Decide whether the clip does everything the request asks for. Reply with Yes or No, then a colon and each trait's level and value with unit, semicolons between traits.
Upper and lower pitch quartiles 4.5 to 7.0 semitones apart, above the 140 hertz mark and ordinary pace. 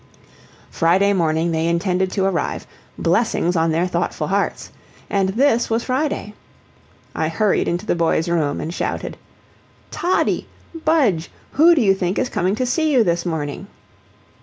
Yes: wide, 5.4 semitones; medium, 185 Hz; average, 150 wpm